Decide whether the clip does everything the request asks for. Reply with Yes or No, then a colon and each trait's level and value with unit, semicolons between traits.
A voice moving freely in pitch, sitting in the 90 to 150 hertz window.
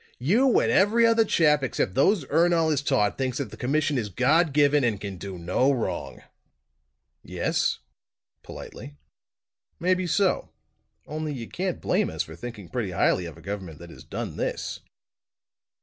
Yes: wide, 8.6 semitones; medium, 140 Hz